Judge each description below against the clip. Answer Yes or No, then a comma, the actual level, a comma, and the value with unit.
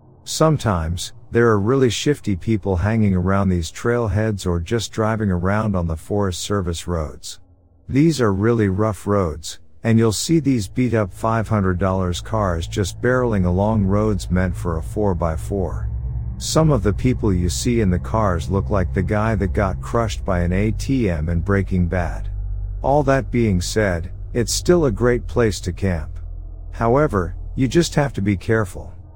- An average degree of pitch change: Yes, average, 4.1 semitones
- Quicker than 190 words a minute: No, average, 165 wpm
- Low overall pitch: Yes, low, 100 Hz